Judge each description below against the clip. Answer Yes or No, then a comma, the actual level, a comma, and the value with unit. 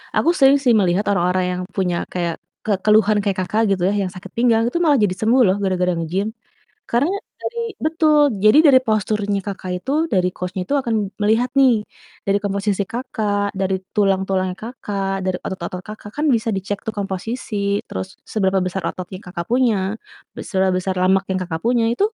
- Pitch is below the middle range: No, high, 200 Hz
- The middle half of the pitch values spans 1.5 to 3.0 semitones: No, average, 3.5 semitones